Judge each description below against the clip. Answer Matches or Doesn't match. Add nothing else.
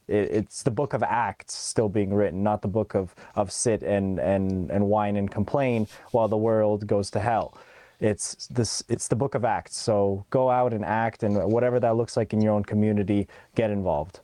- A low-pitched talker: Matches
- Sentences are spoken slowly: Doesn't match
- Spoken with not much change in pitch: Matches